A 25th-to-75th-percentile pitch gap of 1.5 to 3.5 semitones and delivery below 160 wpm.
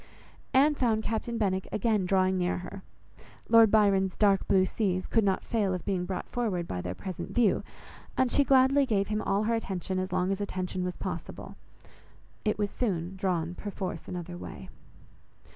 No: average, 3.1 semitones; average, 175 wpm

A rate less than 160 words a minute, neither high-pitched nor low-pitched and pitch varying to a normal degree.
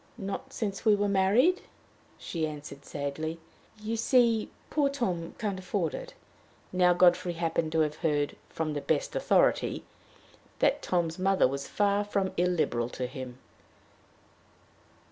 Yes: slow, 135 wpm; medium, 180 Hz; average, 4.8 semitones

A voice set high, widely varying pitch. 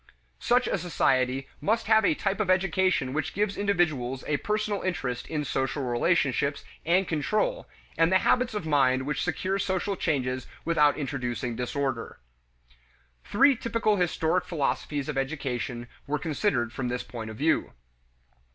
No: medium, 155 Hz; wide, 6.3 semitones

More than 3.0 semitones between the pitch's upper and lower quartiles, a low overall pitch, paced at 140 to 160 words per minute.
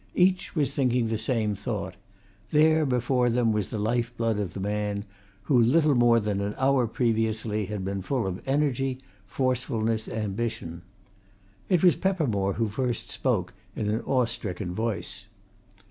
Yes: average, 3.7 semitones; low, 115 Hz; average, 155 wpm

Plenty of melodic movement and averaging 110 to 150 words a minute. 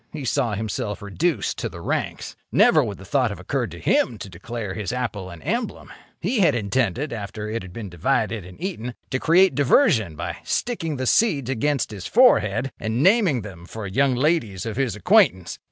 No: wide, 6.5 semitones; average, 190 wpm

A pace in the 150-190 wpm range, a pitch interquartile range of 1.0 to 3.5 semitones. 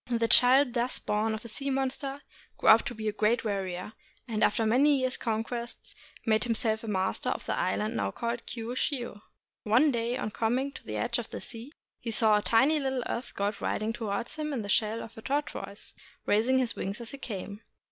No: fast, 205 wpm; average, 3.0 semitones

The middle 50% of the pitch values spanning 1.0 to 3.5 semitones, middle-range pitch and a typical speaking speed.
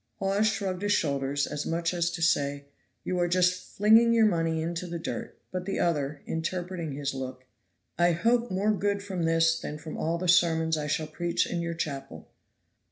Yes: average, 3.1 semitones; medium, 170 Hz; average, 195 wpm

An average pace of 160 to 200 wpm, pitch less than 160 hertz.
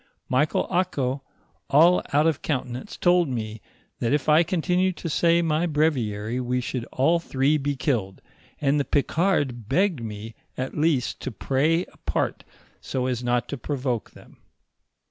No: average, 150 wpm; medium, 140 Hz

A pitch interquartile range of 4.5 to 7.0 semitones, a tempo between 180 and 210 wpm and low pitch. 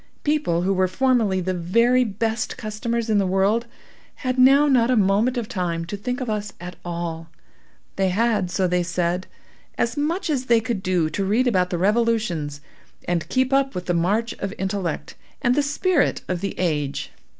No: average, 5.1 semitones; average, 185 wpm; high, 205 Hz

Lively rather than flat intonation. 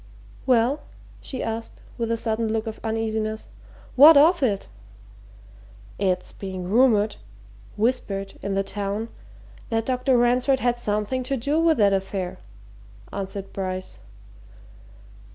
No: average, 4.0 semitones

